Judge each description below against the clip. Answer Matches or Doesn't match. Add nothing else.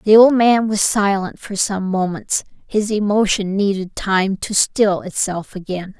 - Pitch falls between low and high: Doesn't match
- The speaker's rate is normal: Matches